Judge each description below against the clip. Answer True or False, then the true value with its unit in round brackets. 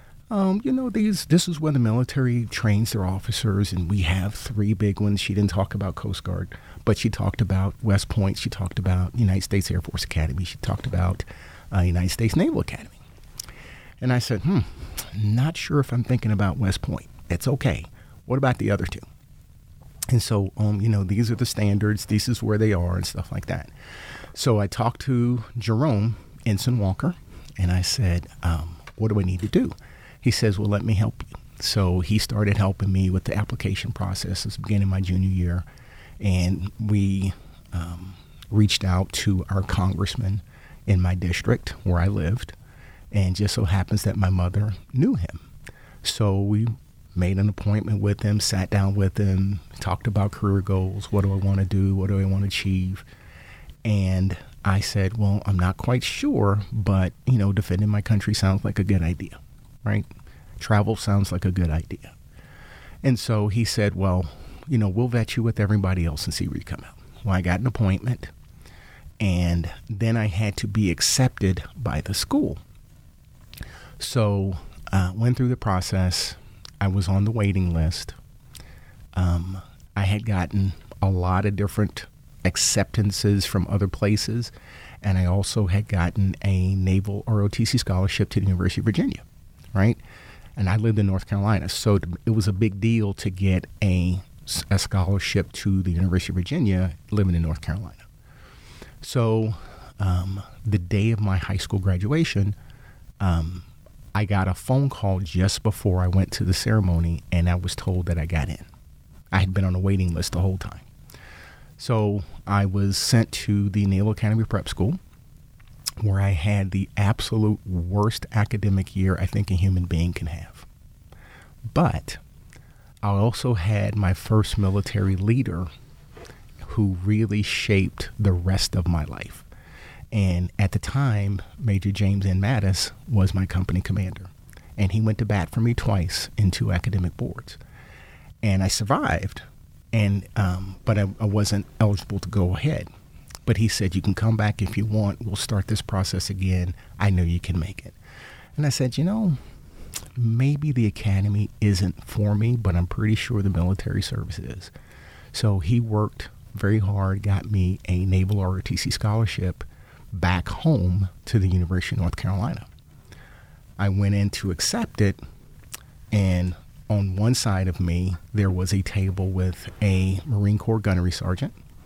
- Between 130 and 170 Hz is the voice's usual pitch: False (100 Hz)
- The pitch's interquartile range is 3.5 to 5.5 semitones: False (2.7 semitones)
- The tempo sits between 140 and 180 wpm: True (175 wpm)